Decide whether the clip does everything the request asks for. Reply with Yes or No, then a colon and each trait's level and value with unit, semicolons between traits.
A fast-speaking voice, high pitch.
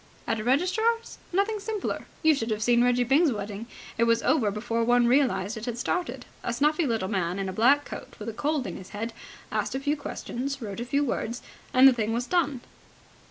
Yes: fast, 215 wpm; high, 245 Hz